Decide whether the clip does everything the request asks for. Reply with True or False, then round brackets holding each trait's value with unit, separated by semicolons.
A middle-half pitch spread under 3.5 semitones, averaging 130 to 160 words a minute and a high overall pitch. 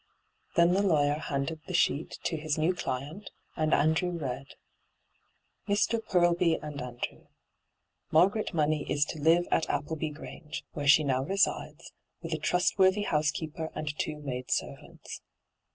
False (2.9 semitones; 150 wpm; 155 Hz)